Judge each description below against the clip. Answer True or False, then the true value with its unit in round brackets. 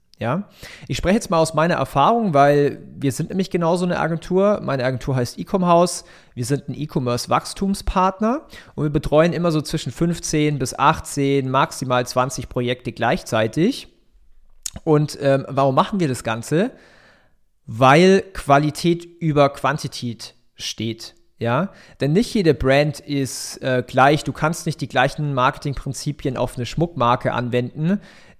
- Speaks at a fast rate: False (140 wpm)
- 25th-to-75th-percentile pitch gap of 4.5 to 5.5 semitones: True (4.8 semitones)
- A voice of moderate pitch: True (145 Hz)